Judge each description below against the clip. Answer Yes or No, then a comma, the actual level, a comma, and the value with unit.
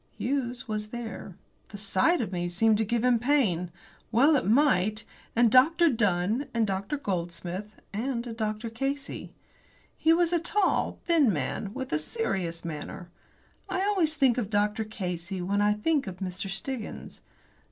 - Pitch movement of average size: No, wide, 6.0 semitones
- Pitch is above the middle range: Yes, high, 220 Hz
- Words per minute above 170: No, average, 160 wpm